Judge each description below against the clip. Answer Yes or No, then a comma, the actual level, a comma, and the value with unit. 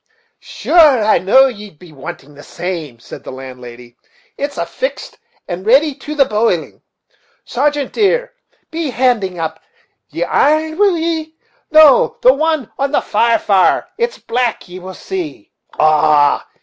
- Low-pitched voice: No, high, 245 Hz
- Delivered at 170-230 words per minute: No, average, 145 wpm